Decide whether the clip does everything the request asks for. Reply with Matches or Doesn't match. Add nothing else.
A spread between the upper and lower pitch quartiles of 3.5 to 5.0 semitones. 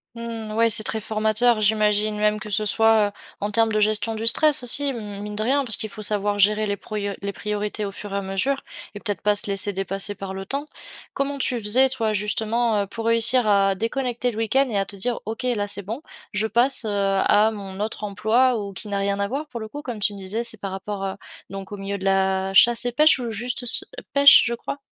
Doesn't match